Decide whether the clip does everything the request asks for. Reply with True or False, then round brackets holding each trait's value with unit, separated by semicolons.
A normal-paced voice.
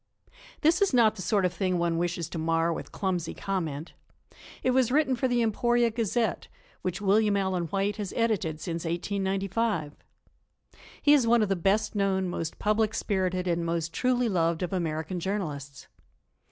True (165 wpm)